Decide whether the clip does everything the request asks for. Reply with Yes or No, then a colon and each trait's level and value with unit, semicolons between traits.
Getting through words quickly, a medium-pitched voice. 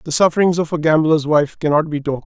Yes: fast, 235 wpm; medium, 155 Hz